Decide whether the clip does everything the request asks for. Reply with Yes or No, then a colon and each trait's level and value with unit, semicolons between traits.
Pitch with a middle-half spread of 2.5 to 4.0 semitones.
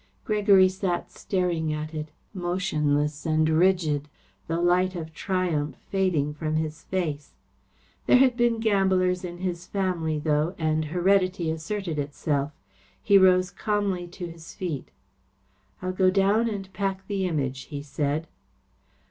Yes: average, 3.6 semitones